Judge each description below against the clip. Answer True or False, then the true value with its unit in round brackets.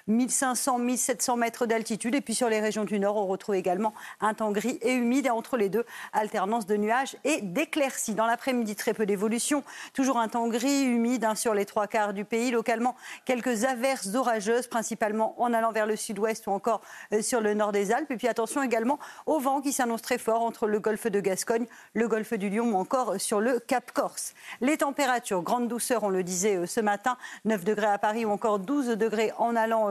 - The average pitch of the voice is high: True (230 Hz)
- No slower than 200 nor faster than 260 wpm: True (210 wpm)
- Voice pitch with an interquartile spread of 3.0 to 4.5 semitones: False (2.6 semitones)